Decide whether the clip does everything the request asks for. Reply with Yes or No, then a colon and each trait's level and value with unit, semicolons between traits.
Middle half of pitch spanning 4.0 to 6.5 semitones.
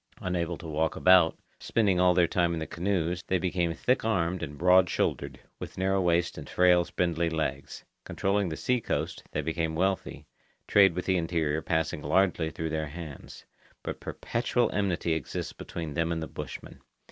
No: narrow, 2.4 semitones